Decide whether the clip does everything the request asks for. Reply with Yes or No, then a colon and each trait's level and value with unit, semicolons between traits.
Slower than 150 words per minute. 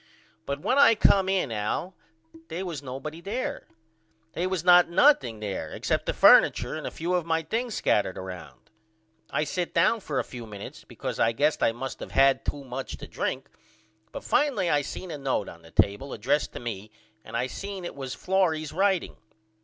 No: average, 190 wpm